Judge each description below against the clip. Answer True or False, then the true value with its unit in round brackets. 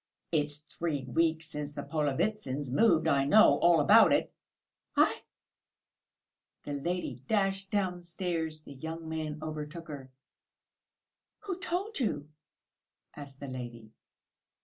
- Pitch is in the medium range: True (155 Hz)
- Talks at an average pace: False (115 wpm)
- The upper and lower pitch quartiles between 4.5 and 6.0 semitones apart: False (3.9 semitones)